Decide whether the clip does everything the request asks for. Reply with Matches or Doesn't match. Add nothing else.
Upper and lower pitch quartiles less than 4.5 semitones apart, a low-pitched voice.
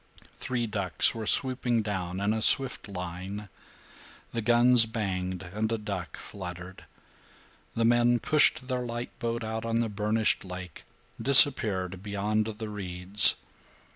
Matches